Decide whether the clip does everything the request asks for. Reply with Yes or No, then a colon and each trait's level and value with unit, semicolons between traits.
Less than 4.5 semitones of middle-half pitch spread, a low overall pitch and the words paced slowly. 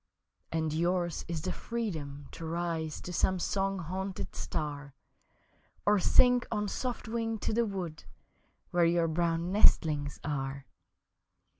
No: average, 3.9 semitones; medium, 170 Hz; slow, 130 wpm